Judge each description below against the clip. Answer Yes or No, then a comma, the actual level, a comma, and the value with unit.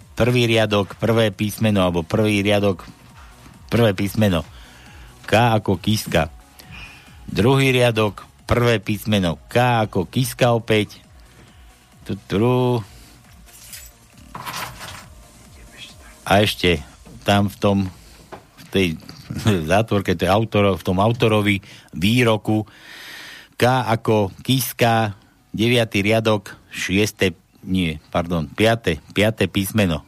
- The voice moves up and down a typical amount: Yes, average, 3.2 semitones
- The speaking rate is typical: No, slow, 90 wpm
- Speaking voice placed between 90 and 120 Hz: Yes, low, 105 Hz